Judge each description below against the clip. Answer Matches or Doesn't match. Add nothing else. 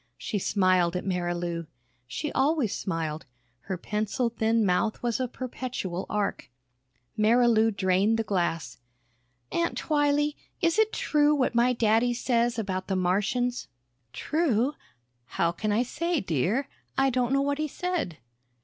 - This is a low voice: Doesn't match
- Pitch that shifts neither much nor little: Doesn't match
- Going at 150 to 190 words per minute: Doesn't match